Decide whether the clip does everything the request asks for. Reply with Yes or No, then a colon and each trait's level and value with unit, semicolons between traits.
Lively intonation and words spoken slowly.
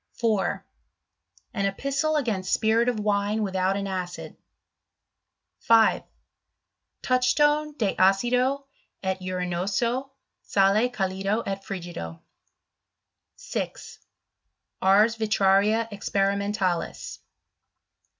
No: average, 3.5 semitones; slow, 80 wpm